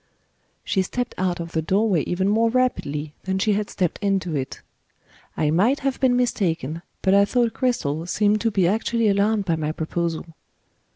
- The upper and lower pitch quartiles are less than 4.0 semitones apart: No, average, 5.1 semitones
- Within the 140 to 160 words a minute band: No, average, 175 wpm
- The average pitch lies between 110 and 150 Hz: No, high, 195 Hz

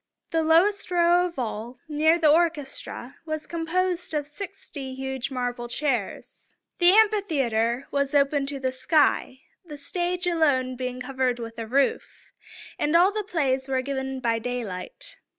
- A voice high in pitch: Yes, very high, 280 Hz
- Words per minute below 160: Yes, average, 150 wpm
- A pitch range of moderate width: Yes, average, 4.8 semitones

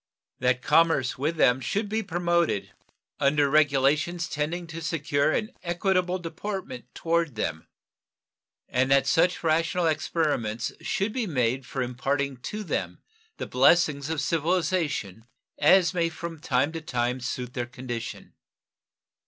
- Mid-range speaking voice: Yes, medium, 155 Hz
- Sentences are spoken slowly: Yes, slow, 130 wpm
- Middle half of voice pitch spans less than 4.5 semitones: No, average, 4.8 semitones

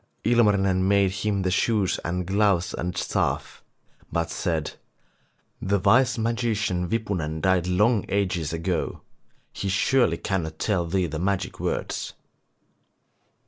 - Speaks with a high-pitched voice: No, very low, 95 Hz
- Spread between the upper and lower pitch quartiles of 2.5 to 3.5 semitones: Yes, average, 3.0 semitones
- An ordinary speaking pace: No, slow, 120 wpm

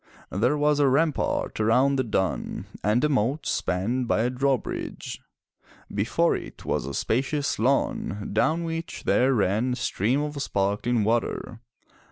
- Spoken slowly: No, average, 150 wpm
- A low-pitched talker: Yes, low, 125 Hz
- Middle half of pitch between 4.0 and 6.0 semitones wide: Yes, average, 4.9 semitones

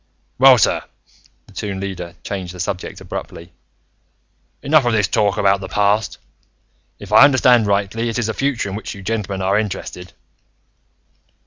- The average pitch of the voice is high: No, low, 105 Hz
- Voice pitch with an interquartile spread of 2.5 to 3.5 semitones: Yes, average, 2.8 semitones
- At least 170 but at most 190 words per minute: No, average, 155 wpm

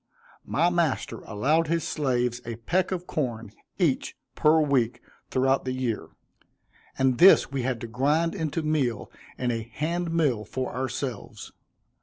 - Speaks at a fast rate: No, average, 145 wpm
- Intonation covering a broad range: No, average, 4.7 semitones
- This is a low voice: Yes, low, 130 Hz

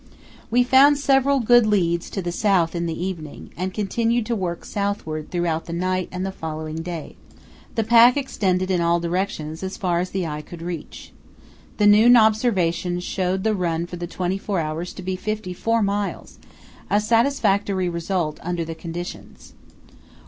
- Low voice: No, medium, 185 Hz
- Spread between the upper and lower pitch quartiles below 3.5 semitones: No, average, 3.8 semitones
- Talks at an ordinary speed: Yes, average, 170 wpm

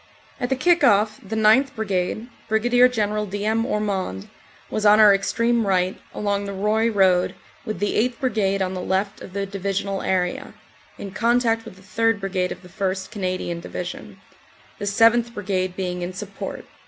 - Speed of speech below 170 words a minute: No, average, 175 wpm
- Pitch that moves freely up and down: No, average, 2.8 semitones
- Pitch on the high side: Yes, high, 200 Hz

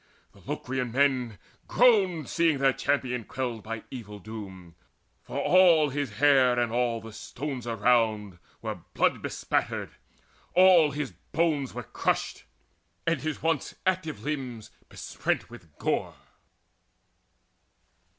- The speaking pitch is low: Yes, low, 130 Hz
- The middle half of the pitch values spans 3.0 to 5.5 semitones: Yes, average, 5.1 semitones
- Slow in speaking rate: Yes, slow, 120 wpm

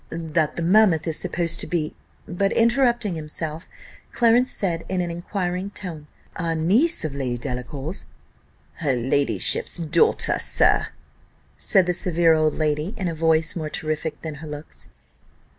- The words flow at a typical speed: Yes, average, 150 wpm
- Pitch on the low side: No, medium, 165 Hz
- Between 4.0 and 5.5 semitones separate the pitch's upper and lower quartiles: No, average, 3.1 semitones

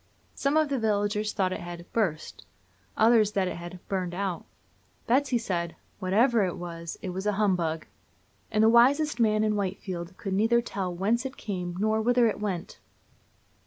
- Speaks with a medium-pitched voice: No, high, 205 Hz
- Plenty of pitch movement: No, average, 3.9 semitones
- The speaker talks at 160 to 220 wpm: Yes, average, 170 wpm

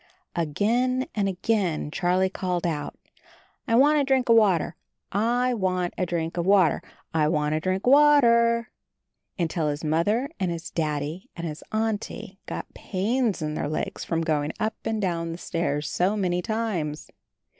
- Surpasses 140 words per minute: Yes, average, 165 wpm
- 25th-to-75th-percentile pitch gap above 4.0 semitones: Yes, wide, 5.5 semitones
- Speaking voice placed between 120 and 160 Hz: No, medium, 185 Hz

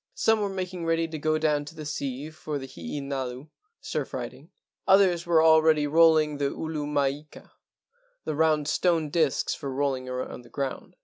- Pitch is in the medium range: Yes, medium, 150 Hz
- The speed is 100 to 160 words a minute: No, average, 180 wpm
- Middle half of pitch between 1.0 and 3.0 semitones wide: Yes, narrow, 2.5 semitones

